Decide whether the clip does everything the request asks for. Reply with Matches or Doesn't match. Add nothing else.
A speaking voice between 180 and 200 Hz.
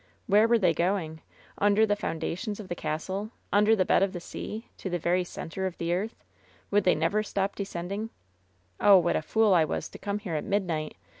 Matches